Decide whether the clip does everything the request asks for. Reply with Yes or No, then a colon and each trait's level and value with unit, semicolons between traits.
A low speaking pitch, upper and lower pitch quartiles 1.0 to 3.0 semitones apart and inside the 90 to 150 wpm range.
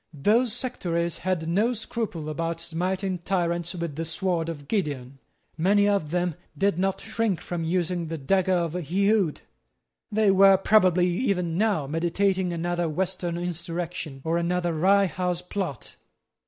No: medium, 175 Hz; average, 2.7 semitones; average, 140 wpm